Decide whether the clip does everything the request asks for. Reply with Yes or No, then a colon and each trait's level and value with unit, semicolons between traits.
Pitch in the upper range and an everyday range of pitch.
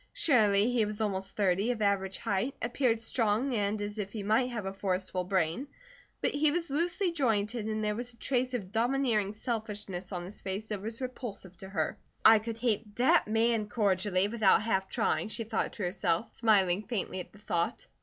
Yes: high, 215 Hz; average, 3.3 semitones